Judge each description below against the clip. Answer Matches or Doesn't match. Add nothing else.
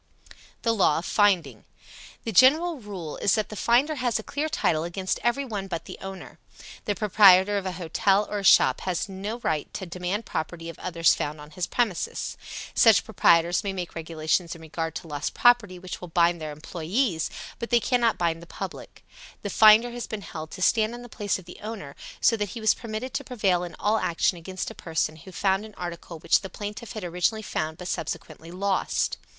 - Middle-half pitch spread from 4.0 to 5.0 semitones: Matches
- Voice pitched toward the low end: Doesn't match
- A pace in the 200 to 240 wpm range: Matches